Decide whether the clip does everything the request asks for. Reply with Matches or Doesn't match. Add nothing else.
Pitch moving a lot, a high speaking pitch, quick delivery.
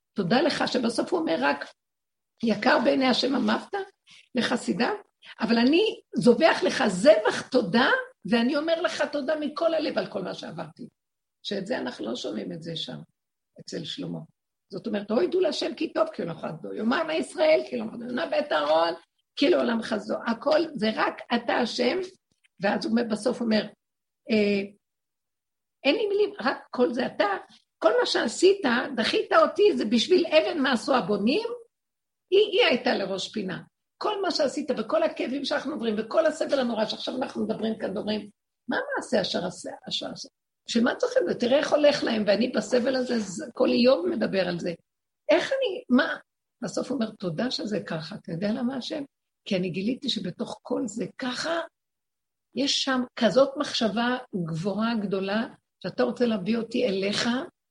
Matches